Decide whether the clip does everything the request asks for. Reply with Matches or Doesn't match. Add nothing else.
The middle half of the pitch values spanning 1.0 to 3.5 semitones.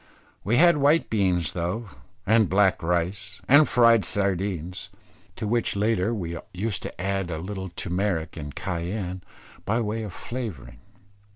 Doesn't match